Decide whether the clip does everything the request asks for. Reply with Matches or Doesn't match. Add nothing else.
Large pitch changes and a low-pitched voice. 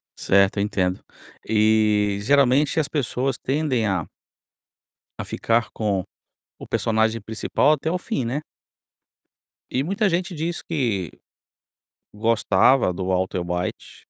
Matches